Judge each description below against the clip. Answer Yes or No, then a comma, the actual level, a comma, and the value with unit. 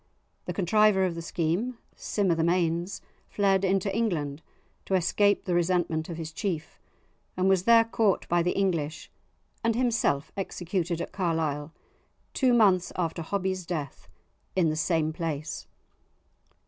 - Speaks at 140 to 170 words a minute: Yes, average, 145 wpm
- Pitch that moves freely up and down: No, average, 3.3 semitones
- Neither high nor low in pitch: Yes, medium, 180 Hz